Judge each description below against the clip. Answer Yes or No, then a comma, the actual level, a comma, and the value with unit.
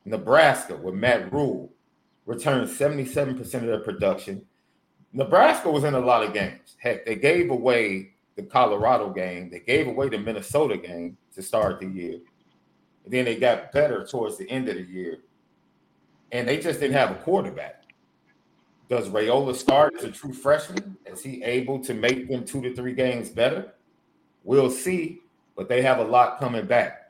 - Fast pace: No, average, 175 wpm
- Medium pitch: No, low, 125 Hz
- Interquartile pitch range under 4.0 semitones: Yes, average, 3.5 semitones